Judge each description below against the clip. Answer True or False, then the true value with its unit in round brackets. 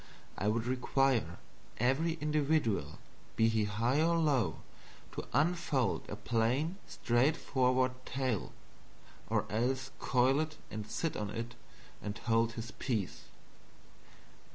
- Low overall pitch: True (125 Hz)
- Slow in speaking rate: True (115 wpm)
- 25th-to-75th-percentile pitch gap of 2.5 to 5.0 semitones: True (4.3 semitones)